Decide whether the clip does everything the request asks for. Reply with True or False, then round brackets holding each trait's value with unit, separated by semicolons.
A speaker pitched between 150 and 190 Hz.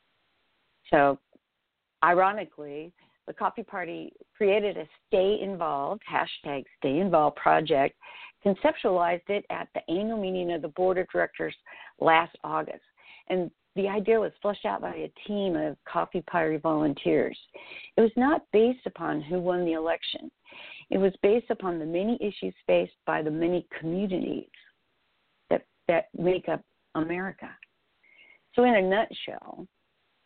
True (185 Hz)